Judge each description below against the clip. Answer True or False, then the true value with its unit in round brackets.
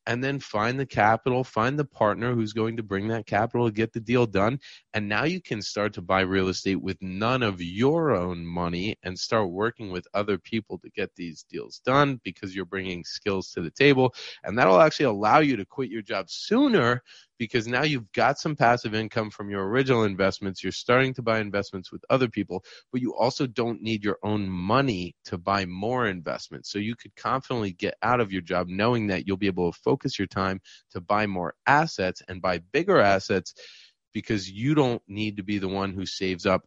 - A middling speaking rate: False (215 wpm)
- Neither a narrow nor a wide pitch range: True (4.4 semitones)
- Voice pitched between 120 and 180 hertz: False (105 Hz)